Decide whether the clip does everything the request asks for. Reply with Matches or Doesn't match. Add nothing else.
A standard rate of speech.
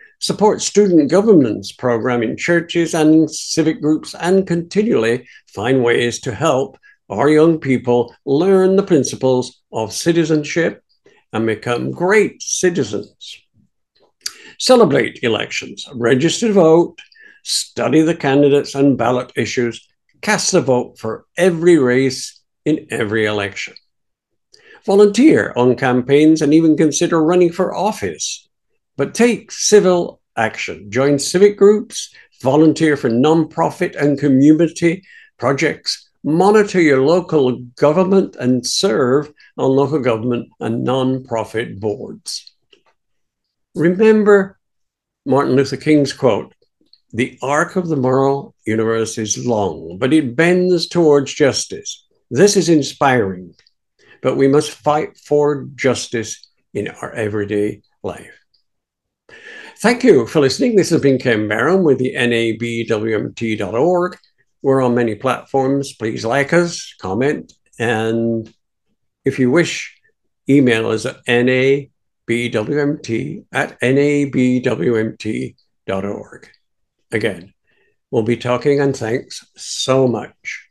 Doesn't match